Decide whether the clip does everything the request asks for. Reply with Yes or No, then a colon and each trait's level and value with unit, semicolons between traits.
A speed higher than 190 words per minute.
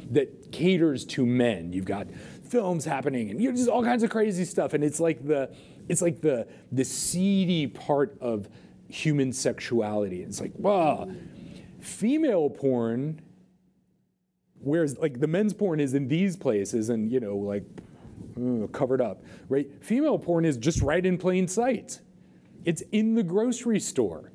No: average, 160 wpm